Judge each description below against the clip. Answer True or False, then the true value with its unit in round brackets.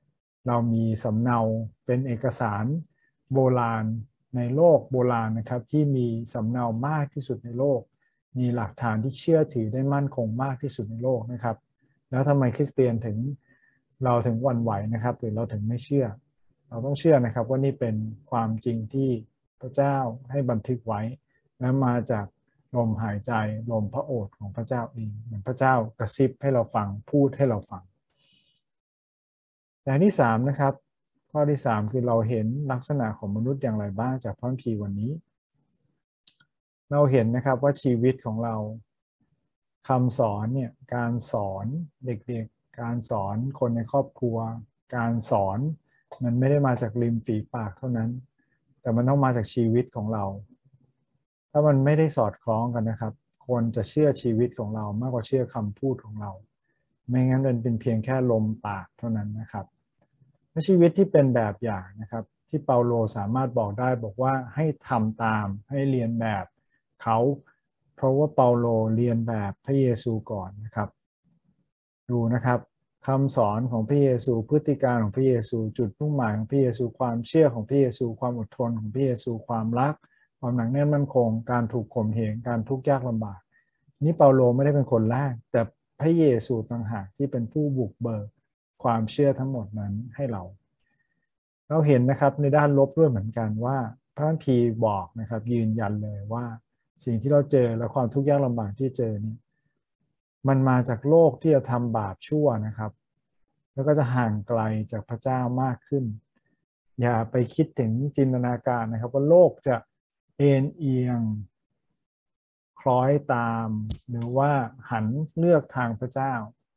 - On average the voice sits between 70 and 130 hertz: True (120 Hz)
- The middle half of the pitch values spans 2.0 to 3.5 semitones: True (3.2 semitones)